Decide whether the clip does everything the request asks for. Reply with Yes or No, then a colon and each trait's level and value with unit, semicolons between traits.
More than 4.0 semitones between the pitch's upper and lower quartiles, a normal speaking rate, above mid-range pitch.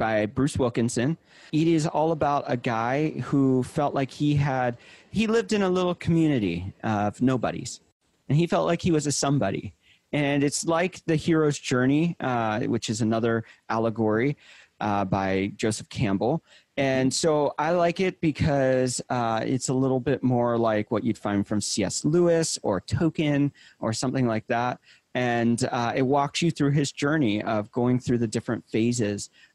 No: average, 4.7 semitones; average, 170 wpm; low, 130 Hz